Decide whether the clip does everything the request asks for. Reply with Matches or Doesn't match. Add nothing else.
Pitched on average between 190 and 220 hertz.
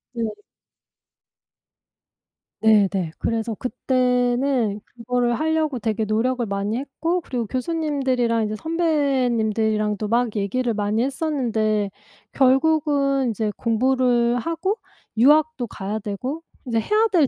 Doesn't match